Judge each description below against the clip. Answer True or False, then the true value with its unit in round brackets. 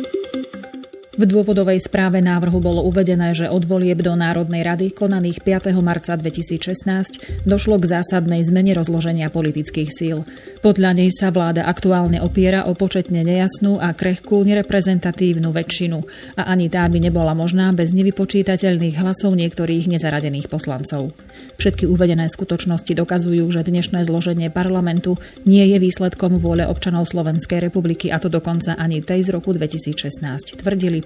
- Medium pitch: True (175 Hz)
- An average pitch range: False (2.0 semitones)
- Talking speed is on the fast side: False (140 wpm)